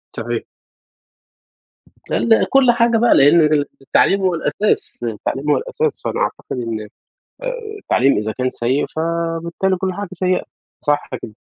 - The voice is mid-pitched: Yes, medium, 170 Hz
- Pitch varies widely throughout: Yes, wide, 7.0 semitones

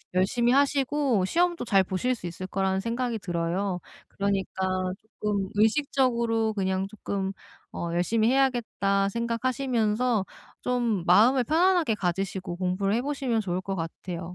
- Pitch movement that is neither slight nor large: Yes, average, 4.7 semitones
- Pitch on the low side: No, high, 210 Hz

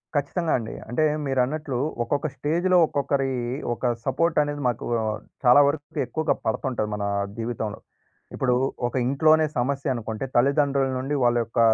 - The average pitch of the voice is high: No, low, 135 Hz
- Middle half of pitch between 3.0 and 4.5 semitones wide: Yes, average, 3.3 semitones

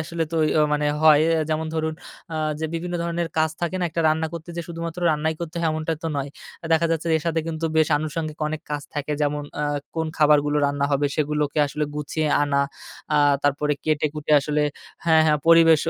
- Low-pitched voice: No, medium, 155 Hz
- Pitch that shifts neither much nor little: No, narrow, 1.6 semitones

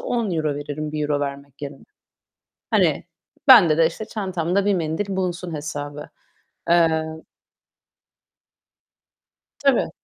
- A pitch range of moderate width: Yes, average, 4.1 semitones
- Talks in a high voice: No, medium, 160 Hz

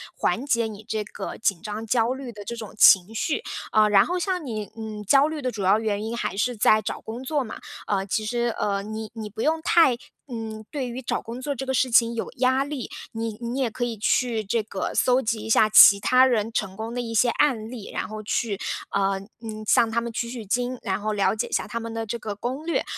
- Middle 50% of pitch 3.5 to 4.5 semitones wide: No, average, 2.7 semitones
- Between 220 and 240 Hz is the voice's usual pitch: Yes, high, 225 Hz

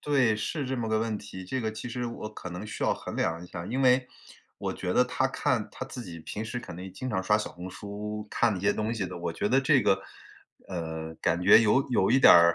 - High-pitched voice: No, low, 105 Hz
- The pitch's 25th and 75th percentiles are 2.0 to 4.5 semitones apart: No, average, 5.2 semitones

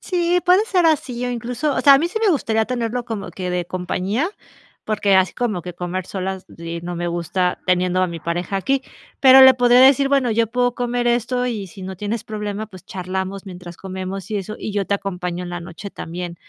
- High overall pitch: Yes, high, 200 Hz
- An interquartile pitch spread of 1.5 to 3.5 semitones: No, average, 5.2 semitones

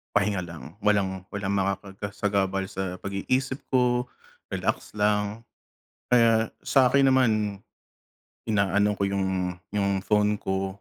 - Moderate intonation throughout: No, narrow, 2.0 semitones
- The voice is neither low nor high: No, low, 100 Hz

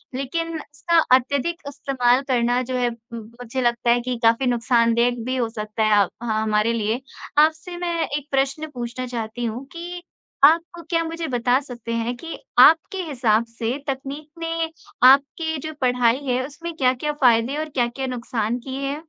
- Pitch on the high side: Yes, very high, 255 Hz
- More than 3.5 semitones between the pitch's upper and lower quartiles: Yes, average, 4.1 semitones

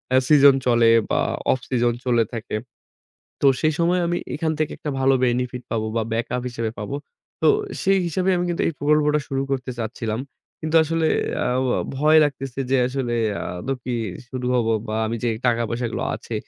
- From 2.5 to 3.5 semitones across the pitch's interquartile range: No, average, 4.2 semitones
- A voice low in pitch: Yes, low, 130 Hz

